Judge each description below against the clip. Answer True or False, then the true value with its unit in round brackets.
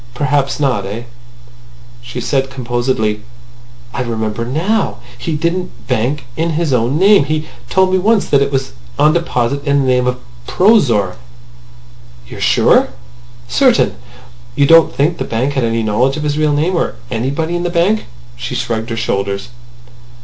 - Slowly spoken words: False (165 wpm)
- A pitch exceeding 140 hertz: False (135 Hz)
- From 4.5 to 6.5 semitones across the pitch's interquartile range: True (5.5 semitones)